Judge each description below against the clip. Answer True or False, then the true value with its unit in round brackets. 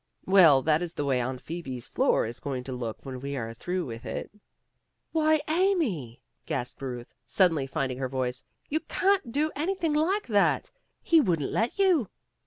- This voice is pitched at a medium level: True (160 Hz)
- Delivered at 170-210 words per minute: True (175 wpm)